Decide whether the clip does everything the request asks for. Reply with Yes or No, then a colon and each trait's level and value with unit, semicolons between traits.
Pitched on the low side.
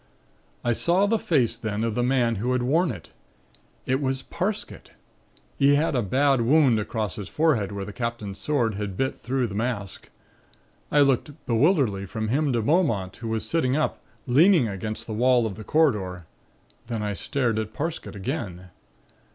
Yes: low, 120 Hz